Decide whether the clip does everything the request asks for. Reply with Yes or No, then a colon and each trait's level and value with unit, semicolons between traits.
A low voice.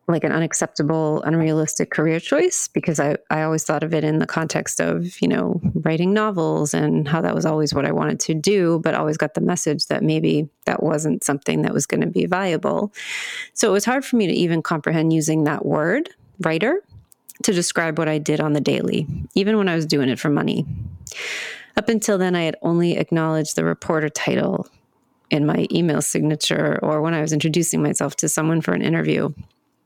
No: medium, 160 Hz